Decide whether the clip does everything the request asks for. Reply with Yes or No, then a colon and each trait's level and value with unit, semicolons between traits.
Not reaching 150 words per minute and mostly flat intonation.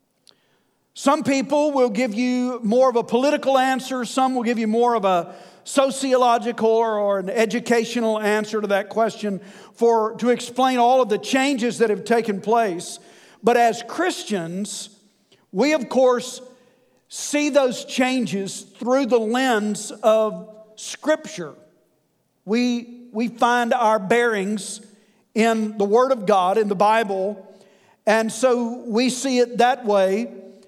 No: slow, 135 wpm; average, 3.2 semitones